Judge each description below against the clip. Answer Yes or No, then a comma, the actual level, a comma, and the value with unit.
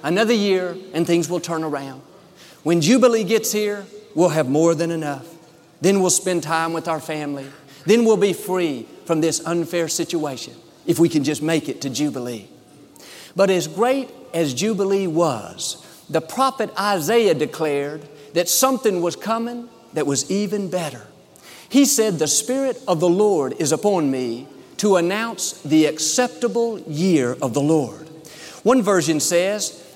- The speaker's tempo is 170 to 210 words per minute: No, average, 155 wpm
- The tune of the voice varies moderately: Yes, average, 4.7 semitones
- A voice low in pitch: No, medium, 170 Hz